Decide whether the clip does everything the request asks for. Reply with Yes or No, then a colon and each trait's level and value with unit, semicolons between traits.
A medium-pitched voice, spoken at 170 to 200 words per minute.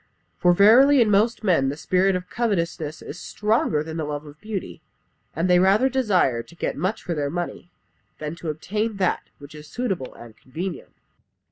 Yes: medium, 180 Hz; average, 180 wpm